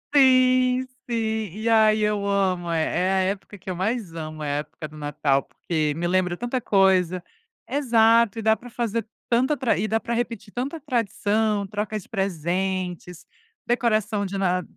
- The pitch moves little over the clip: No, average, 4.3 semitones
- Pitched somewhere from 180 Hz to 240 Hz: Yes, high, 205 Hz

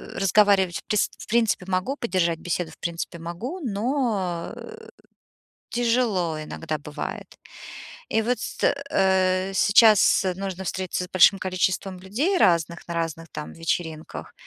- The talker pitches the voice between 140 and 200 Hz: Yes, medium, 185 Hz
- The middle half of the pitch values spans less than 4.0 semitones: No, average, 4.3 semitones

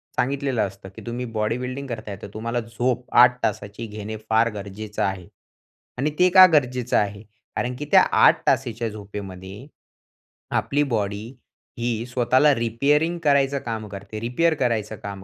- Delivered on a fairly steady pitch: No, average, 3.4 semitones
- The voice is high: No, low, 115 Hz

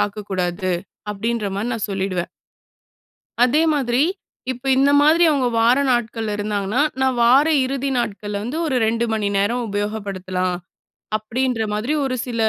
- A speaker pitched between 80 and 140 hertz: No, high, 225 Hz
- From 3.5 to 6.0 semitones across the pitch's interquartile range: Yes, average, 3.9 semitones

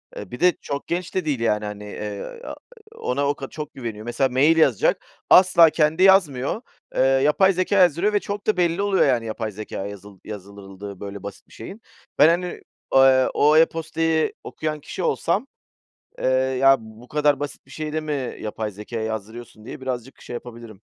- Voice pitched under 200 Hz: Yes, low, 135 Hz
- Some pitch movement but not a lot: No, wide, 6.6 semitones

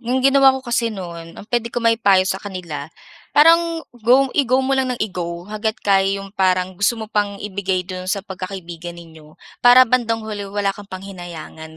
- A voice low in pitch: No, high, 200 Hz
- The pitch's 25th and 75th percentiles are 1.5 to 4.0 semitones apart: No, average, 4.5 semitones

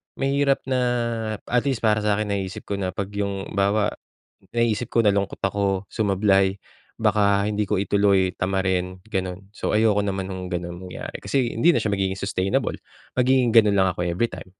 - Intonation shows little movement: Yes, narrow, 2.1 semitones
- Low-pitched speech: Yes, low, 100 Hz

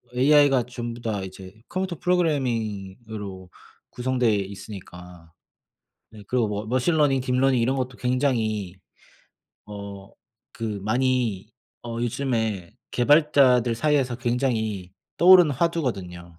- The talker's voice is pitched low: Yes, low, 120 Hz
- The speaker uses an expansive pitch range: No, average, 4.5 semitones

